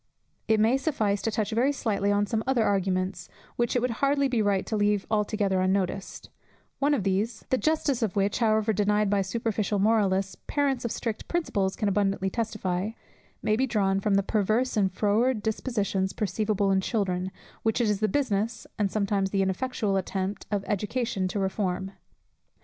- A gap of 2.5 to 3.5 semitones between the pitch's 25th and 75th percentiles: Yes, average, 2.8 semitones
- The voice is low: No, high, 210 Hz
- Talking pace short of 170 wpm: No, average, 175 wpm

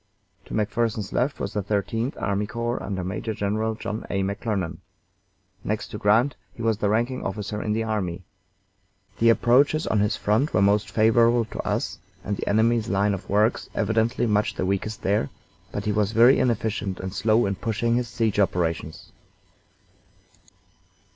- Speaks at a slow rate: No, average, 165 wpm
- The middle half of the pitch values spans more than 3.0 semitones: No, narrow, 2.4 semitones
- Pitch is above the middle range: No, low, 105 Hz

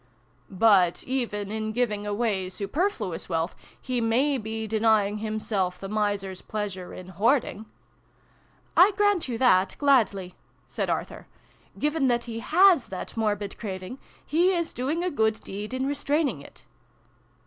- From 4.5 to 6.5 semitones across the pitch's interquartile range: Yes, average, 5.0 semitones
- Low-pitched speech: No, high, 220 Hz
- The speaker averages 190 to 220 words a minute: No, average, 170 wpm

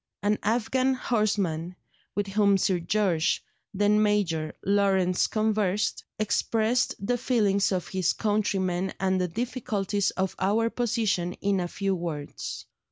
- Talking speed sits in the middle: No, slow, 125 wpm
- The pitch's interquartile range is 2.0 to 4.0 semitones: Yes, narrow, 2.6 semitones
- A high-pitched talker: Yes, high, 200 Hz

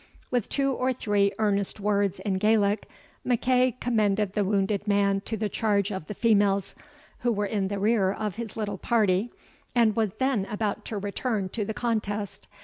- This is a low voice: No, high, 210 Hz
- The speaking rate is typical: Yes, average, 175 wpm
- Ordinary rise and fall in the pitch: No, narrow, 2.1 semitones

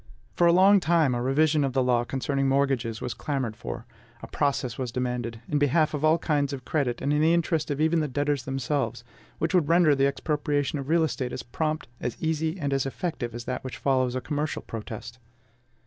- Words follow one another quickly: Yes, fast, 210 wpm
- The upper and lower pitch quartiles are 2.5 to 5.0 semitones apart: Yes, average, 3.6 semitones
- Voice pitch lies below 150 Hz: Yes, medium, 140 Hz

